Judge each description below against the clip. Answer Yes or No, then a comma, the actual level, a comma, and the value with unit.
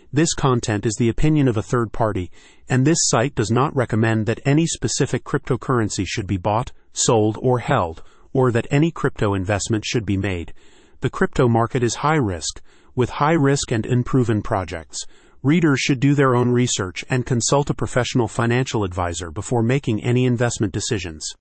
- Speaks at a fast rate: No, average, 175 wpm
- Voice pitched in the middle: No, low, 120 Hz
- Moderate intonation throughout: Yes, average, 3.8 semitones